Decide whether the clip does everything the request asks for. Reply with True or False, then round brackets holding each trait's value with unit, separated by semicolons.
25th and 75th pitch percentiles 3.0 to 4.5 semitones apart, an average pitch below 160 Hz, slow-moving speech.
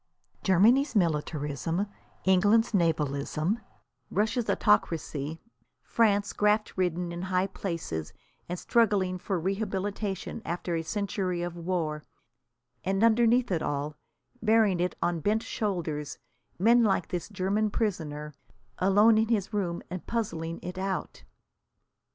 False (3.9 semitones; 185 Hz; 115 wpm)